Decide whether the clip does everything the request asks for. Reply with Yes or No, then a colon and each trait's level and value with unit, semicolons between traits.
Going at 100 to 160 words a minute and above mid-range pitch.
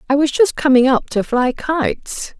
No: average, 200 wpm; very high, 275 Hz